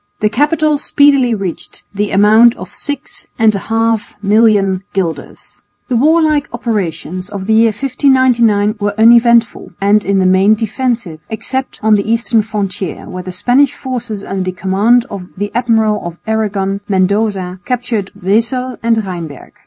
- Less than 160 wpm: Yes, average, 150 wpm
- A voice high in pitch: Yes, high, 220 Hz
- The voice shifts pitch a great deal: No, average, 3.5 semitones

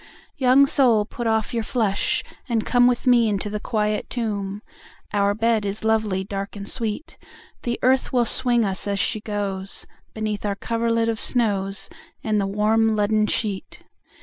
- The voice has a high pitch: Yes, high, 215 Hz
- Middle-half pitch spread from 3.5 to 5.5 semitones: No, narrow, 2.4 semitones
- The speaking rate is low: No, average, 170 wpm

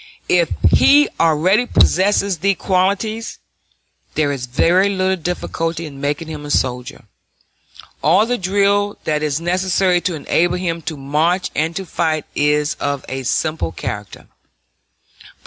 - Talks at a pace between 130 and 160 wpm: Yes, slow, 135 wpm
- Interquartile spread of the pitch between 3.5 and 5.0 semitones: Yes, average, 4.1 semitones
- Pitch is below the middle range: No, medium, 170 Hz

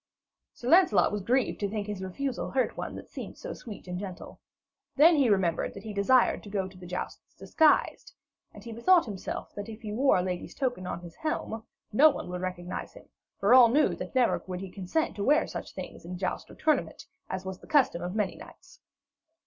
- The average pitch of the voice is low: No, high, 210 Hz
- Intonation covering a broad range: Yes, wide, 6.0 semitones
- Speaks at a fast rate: Yes, fast, 215 wpm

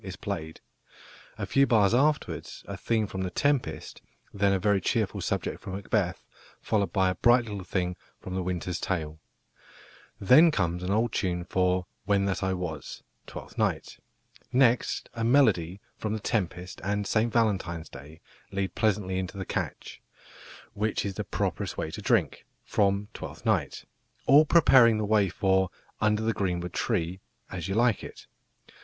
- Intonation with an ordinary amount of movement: Yes, average, 3.3 semitones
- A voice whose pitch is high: No, low, 100 Hz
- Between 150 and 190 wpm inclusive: Yes, average, 160 wpm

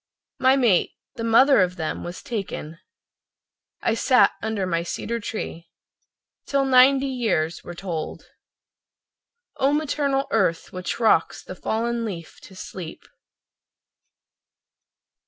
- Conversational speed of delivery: No, slow, 115 wpm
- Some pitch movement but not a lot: No, wide, 6.7 semitones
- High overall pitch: Yes, high, 220 Hz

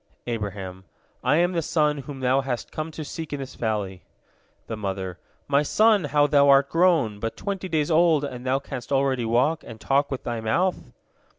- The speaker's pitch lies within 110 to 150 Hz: Yes, medium, 140 Hz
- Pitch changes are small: No, average, 5.1 semitones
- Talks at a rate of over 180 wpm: Yes, average, 190 wpm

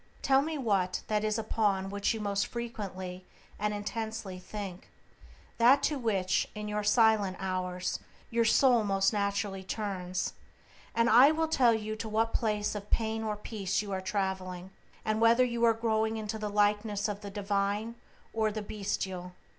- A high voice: Yes, high, 210 Hz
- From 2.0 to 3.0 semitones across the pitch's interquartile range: Yes, narrow, 2.4 semitones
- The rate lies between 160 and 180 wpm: Yes, average, 165 wpm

